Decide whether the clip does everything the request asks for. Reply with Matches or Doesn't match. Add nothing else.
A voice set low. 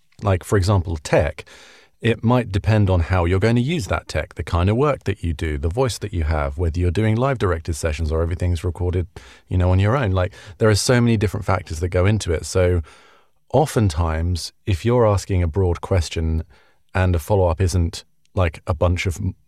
Matches